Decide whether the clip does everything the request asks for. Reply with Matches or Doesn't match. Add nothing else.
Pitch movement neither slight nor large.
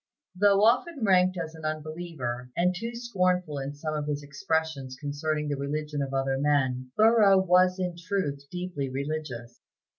Matches